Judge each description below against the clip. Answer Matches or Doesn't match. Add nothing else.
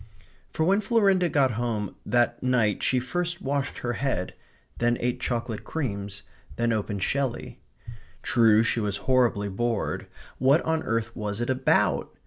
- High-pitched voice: Doesn't match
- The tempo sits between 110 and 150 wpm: Matches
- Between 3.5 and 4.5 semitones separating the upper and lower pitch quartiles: Matches